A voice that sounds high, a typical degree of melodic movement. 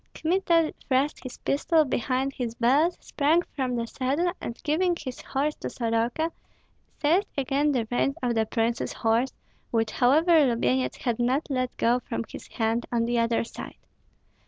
Yes: very high, 255 Hz; average, 4.4 semitones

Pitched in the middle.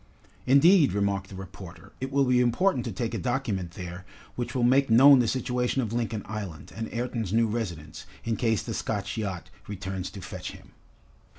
No: low, 115 Hz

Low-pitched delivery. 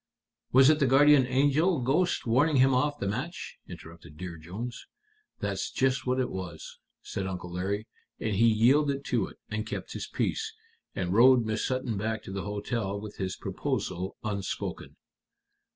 Yes: low, 115 Hz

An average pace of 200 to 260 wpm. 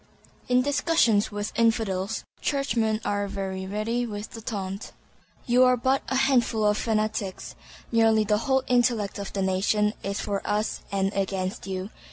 No: average, 155 wpm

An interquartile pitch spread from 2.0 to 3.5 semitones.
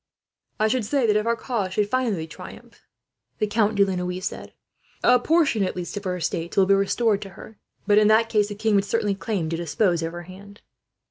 Yes: average, 3.0 semitones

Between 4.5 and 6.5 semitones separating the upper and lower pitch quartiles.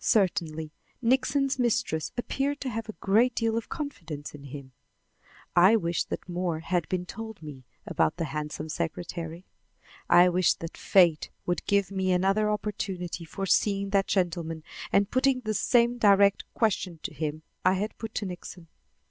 Yes: average, 4.9 semitones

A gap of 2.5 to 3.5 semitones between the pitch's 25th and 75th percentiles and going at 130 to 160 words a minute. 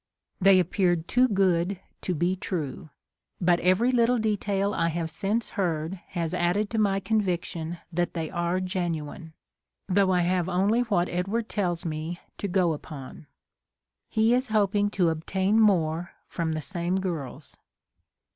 Yes: average, 3.1 semitones; average, 145 wpm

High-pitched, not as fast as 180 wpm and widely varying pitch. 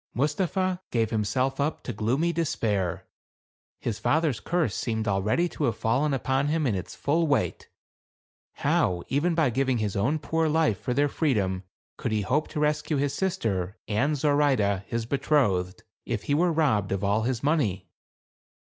No: low, 130 Hz; average, 165 wpm; wide, 6.1 semitones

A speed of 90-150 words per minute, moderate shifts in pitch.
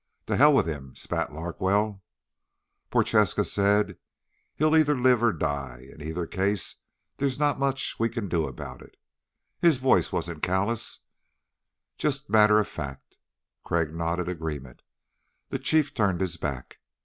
No: average, 140 wpm; wide, 7.7 semitones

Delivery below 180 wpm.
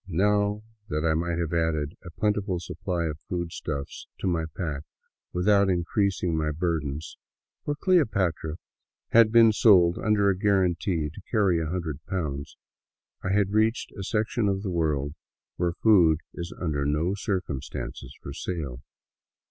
Yes: average, 160 wpm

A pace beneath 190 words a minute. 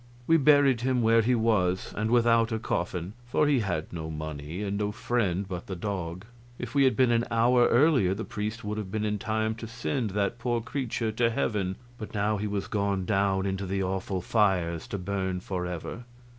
No: average, 200 wpm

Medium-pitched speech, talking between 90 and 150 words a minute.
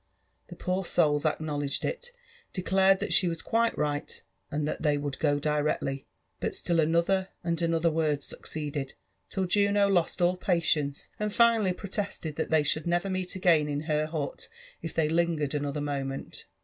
No: medium, 160 Hz; average, 165 wpm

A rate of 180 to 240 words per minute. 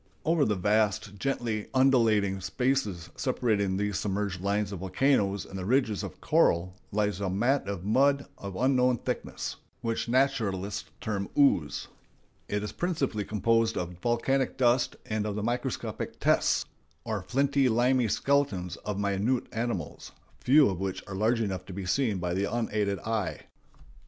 No: average, 150 wpm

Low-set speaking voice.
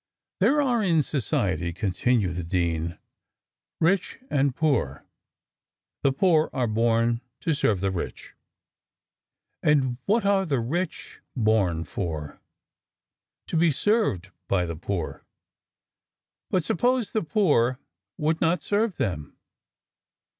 Yes: low, 130 Hz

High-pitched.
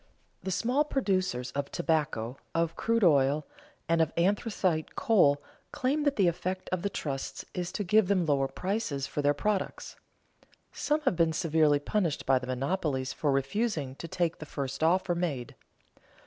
No: medium, 165 Hz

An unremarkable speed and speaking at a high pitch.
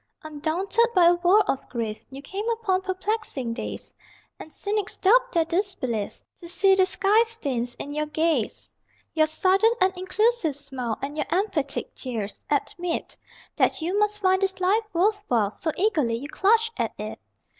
Yes: average, 165 wpm; very high, 360 Hz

